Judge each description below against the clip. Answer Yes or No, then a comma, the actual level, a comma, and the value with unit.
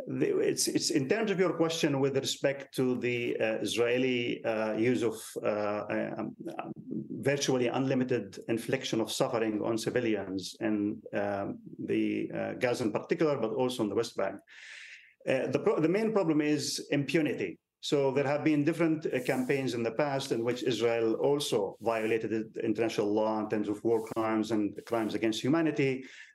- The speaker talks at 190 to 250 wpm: No, average, 165 wpm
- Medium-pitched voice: No, low, 120 Hz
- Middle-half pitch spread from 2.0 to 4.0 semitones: No, average, 4.4 semitones